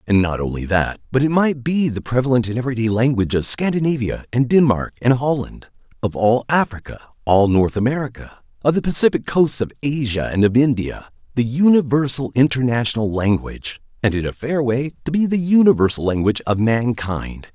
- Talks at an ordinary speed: Yes, average, 170 wpm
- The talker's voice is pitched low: Yes, low, 125 Hz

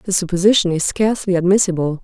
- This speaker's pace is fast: No, average, 145 wpm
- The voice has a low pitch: No, medium, 185 Hz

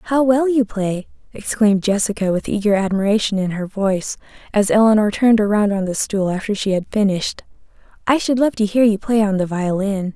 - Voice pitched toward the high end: Yes, high, 210 Hz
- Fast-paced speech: No, average, 195 wpm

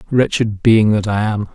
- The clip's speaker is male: Yes, male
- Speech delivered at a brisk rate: No, average, 195 wpm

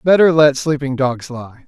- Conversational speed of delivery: Yes, average, 180 wpm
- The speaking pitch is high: No, medium, 140 Hz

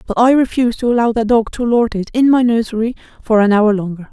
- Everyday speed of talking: No, fast, 250 wpm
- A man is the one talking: No, female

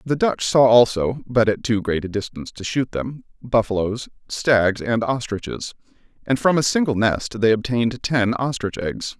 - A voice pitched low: Yes, low, 115 Hz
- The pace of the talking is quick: No, average, 175 wpm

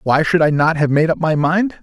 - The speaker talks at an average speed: No, fast, 295 wpm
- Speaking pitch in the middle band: Yes, medium, 160 Hz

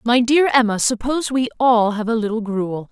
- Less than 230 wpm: Yes, fast, 205 wpm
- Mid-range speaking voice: No, high, 230 Hz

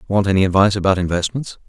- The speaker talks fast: No, average, 180 wpm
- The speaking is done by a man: Yes, male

